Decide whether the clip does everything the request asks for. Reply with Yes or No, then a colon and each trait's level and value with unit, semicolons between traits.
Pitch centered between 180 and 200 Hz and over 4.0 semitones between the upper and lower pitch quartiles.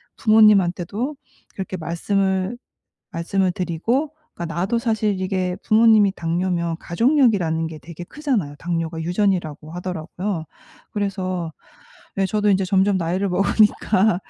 No: medium, 185 Hz; average, 3.4 semitones